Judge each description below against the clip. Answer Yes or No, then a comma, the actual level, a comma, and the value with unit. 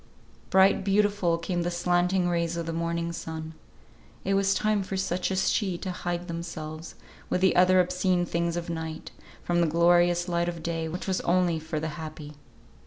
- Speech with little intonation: Yes, narrow, 1.6 semitones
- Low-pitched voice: No, medium, 175 Hz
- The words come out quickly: No, average, 180 wpm